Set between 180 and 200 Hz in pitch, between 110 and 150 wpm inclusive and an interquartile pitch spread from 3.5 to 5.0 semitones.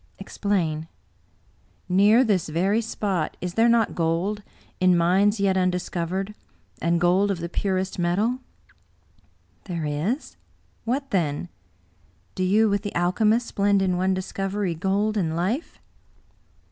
No: high, 190 Hz; average, 145 wpm; average, 2.9 semitones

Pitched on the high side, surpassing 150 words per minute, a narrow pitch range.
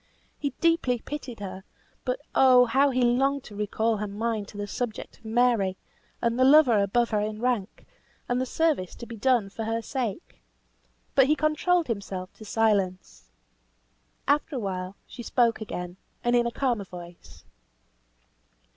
No: high, 230 Hz; average, 160 wpm; average, 4.0 semitones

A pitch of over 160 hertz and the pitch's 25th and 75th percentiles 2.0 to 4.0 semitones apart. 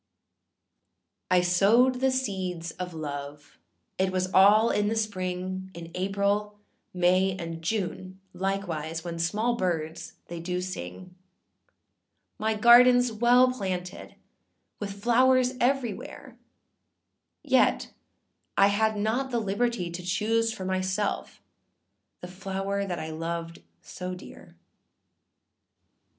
Yes: high, 190 Hz; average, 3.6 semitones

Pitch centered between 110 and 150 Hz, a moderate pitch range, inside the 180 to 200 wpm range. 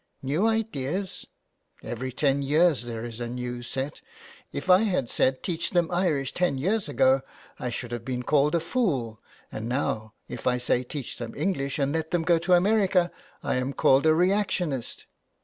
No: medium, 140 Hz; wide, 5.9 semitones; average, 185 wpm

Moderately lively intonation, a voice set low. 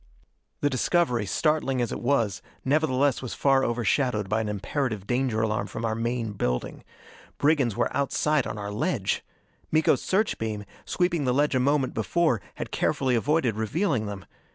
Yes: average, 4.7 semitones; low, 125 Hz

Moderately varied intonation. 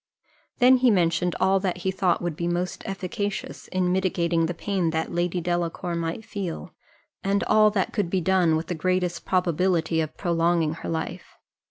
No: narrow, 2.1 semitones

